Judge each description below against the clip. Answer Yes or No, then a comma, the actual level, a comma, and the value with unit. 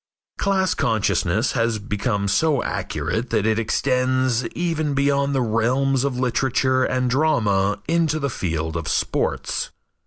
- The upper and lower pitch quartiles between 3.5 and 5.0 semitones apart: Yes, average, 4.4 semitones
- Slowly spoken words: Yes, slow, 130 wpm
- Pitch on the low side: Yes, low, 125 Hz